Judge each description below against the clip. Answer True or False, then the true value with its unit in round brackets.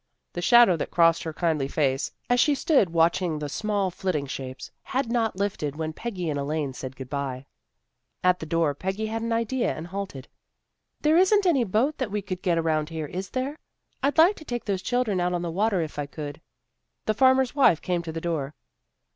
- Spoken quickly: True (210 wpm)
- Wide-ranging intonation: True (6.8 semitones)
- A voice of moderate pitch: True (180 Hz)